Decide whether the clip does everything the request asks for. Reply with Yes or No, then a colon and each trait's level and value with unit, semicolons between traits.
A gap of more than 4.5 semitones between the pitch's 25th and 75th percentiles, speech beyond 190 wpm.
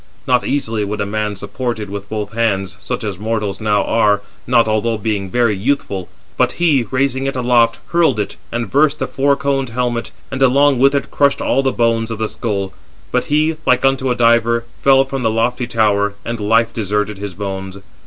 No: average, 4.1 semitones; average, 200 wpm